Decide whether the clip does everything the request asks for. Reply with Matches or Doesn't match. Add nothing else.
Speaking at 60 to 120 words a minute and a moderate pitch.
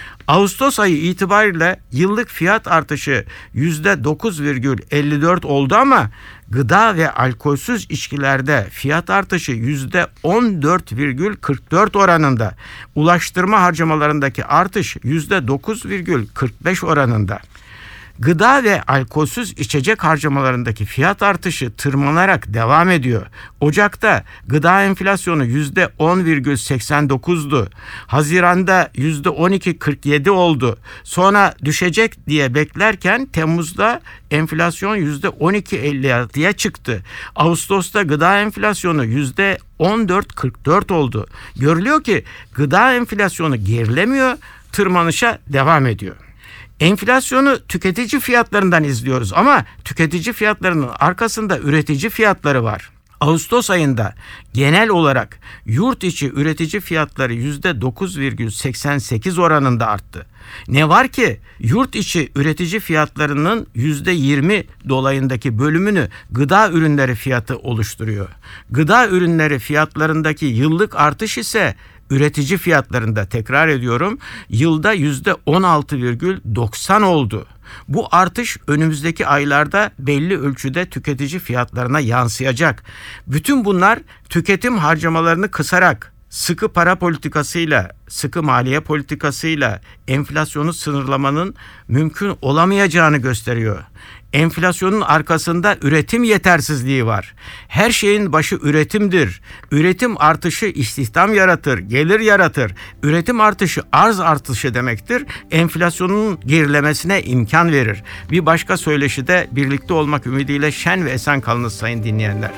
Matches